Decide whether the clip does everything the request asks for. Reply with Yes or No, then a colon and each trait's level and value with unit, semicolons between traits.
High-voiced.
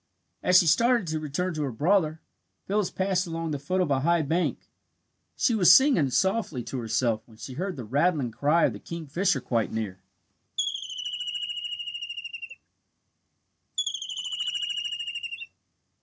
No: medium, 160 Hz